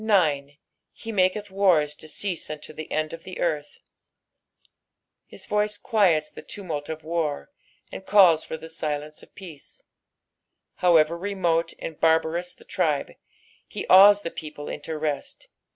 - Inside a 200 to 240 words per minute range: No, average, 140 wpm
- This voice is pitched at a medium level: Yes, medium, 165 Hz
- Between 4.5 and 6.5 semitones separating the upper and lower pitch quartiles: No, average, 3.7 semitones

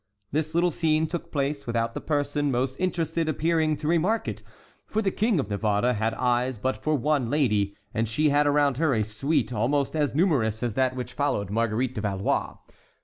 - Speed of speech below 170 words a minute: No, average, 195 wpm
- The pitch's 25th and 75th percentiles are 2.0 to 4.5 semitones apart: No, average, 5.2 semitones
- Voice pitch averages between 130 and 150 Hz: Yes, medium, 140 Hz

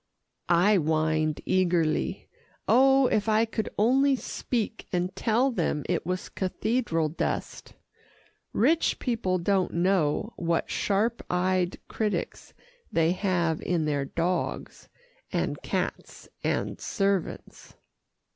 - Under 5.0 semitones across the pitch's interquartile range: Yes, average, 4.6 semitones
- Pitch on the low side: No, medium, 185 Hz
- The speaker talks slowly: Yes, slow, 110 wpm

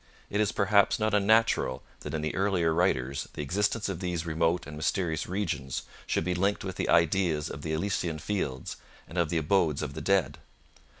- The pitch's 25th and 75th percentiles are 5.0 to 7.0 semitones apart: No, average, 4.2 semitones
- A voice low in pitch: Yes, very low, 85 Hz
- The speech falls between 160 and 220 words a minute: Yes, average, 190 wpm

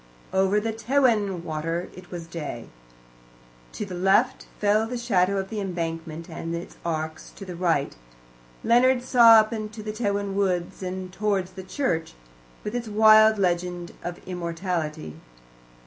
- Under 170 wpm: Yes, average, 145 wpm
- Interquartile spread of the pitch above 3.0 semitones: Yes, average, 3.9 semitones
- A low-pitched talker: No, high, 190 Hz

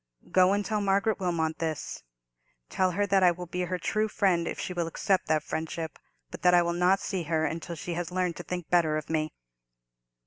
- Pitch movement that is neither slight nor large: No, narrow, 2.3 semitones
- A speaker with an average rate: No, fast, 215 wpm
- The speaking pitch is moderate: Yes, medium, 175 Hz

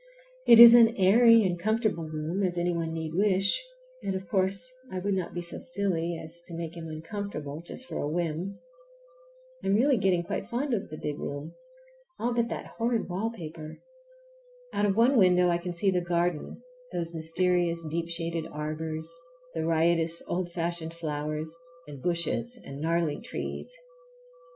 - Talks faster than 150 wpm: Yes, average, 170 wpm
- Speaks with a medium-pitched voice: Yes, medium, 175 Hz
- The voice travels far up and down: No, average, 3.4 semitones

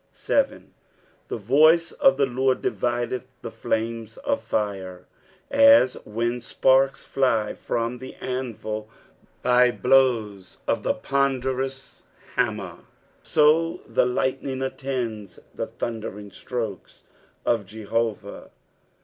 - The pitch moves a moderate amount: Yes, average, 3.5 semitones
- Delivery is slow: Yes, slow, 105 wpm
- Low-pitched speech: Yes, low, 125 Hz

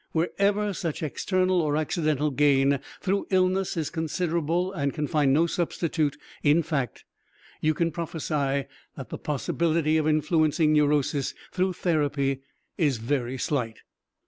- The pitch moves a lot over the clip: No, average, 3.0 semitones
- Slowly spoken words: Yes, slow, 130 wpm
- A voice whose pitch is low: No, medium, 155 Hz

